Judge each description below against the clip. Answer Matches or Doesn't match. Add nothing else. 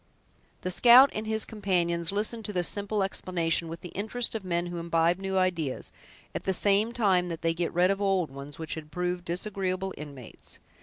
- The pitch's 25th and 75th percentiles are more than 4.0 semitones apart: Doesn't match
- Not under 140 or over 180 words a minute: Doesn't match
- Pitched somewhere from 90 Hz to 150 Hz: Doesn't match